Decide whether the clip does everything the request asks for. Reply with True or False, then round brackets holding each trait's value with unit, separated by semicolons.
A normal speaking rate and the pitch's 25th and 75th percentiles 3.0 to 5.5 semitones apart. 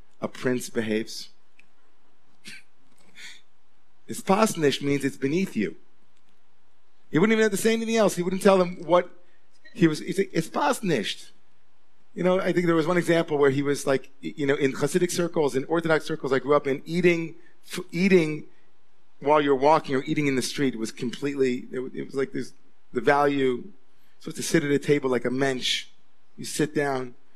True (180 wpm; 4.6 semitones)